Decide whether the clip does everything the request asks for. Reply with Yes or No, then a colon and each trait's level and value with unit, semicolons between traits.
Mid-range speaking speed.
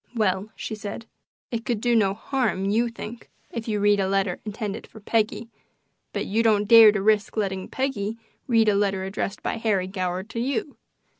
Yes: average, 190 wpm